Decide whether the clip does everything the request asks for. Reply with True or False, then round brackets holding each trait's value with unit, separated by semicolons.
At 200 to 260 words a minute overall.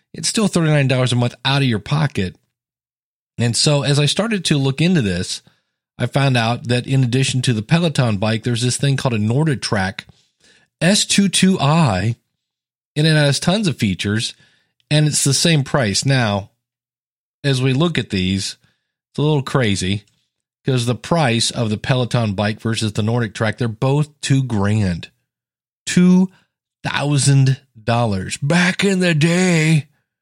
False (155 wpm)